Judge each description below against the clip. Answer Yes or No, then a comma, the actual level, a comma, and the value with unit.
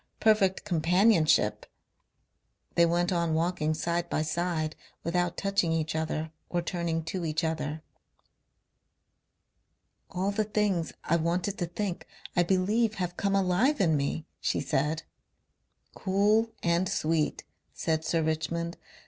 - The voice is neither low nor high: Yes, medium, 170 Hz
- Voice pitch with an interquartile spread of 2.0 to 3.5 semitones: Yes, average, 3.0 semitones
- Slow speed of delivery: Yes, slow, 125 wpm